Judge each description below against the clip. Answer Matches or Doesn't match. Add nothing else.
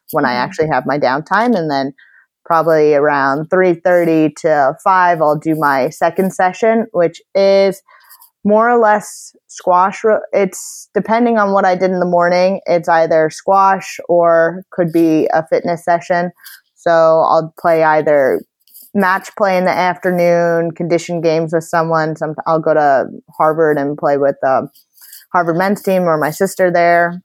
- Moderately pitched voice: Matches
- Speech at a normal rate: Matches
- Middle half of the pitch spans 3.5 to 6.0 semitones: Doesn't match